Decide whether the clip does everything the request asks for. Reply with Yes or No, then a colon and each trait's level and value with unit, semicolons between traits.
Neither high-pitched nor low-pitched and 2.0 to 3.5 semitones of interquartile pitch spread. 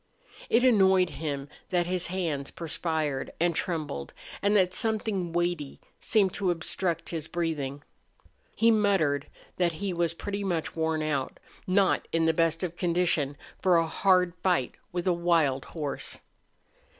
Yes: medium, 170 Hz; average, 2.8 semitones